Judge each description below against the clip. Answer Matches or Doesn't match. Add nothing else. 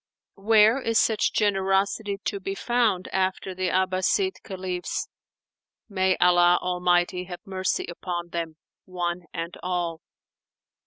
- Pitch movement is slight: Matches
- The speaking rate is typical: Doesn't match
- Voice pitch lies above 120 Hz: Matches